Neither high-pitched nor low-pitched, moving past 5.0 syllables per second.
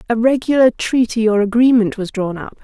No: high, 230 Hz; 5.4 syllables/s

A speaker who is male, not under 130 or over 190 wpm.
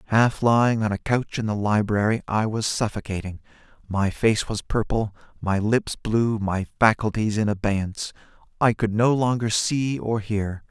Yes: male; average, 160 wpm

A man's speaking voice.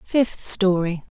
No: female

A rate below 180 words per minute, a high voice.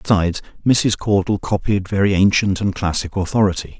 No: average, 140 wpm; low, 100 Hz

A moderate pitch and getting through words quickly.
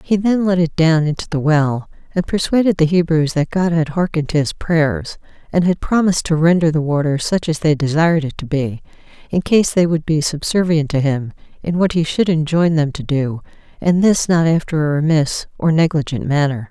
Yes: medium, 160 Hz; fast, 210 wpm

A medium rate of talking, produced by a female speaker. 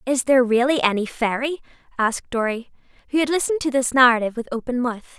Yes: average, 185 wpm; female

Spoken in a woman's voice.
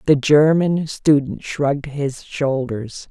Yes: female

